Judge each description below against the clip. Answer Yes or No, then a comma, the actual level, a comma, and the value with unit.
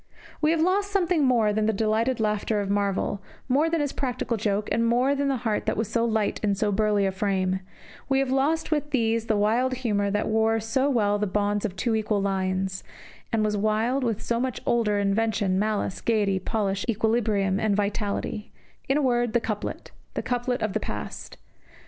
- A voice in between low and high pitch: No, high, 220 Hz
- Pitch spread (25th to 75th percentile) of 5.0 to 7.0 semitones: No, average, 3.3 semitones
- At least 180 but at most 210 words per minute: Yes, average, 195 wpm